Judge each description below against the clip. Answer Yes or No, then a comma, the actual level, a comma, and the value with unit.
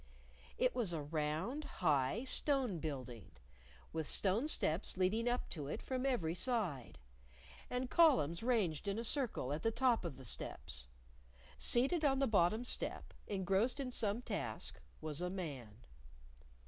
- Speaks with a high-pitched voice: Yes, high, 195 Hz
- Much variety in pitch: Yes, wide, 8.1 semitones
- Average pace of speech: Yes, average, 150 wpm